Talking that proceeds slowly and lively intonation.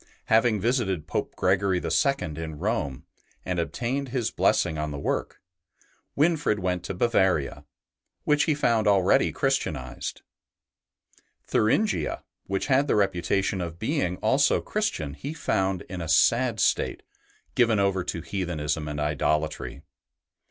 Yes: slow, 130 wpm; wide, 6.3 semitones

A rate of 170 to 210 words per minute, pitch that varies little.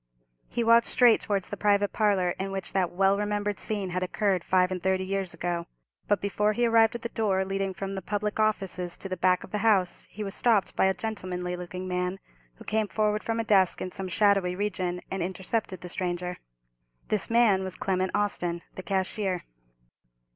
Yes: average, 200 wpm; narrow, 2.3 semitones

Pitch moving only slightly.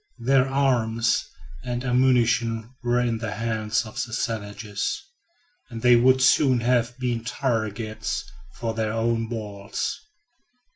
Yes: narrow, 1.8 semitones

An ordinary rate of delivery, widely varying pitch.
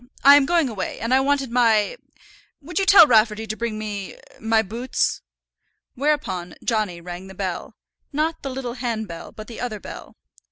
No: average, 170 wpm; average, 4.4 semitones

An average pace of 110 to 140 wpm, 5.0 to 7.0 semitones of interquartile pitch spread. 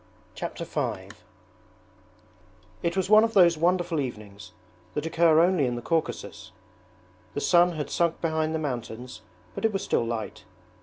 No: average, 150 wpm; wide, 5.4 semitones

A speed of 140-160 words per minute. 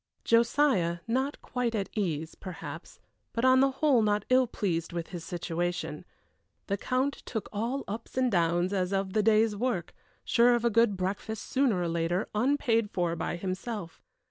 No: average, 170 wpm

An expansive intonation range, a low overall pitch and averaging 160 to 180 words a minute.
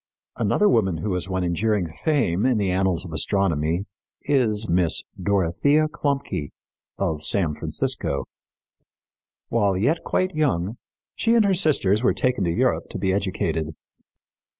No: wide, 7.0 semitones; low, 100 Hz; average, 140 wpm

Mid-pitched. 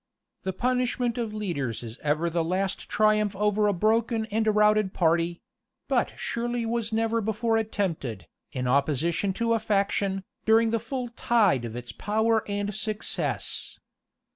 No: high, 210 Hz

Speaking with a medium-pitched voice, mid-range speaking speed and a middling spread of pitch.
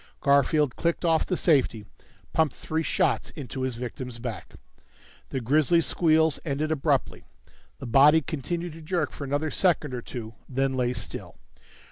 Yes: medium, 145 Hz; average, 150 wpm; average, 3.7 semitones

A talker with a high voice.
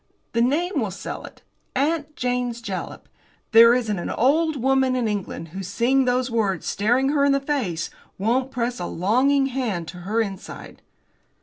Yes: high, 245 Hz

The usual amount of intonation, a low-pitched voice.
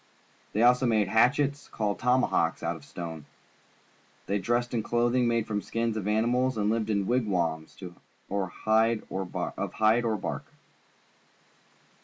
Yes: average, 3.3 semitones; low, 110 Hz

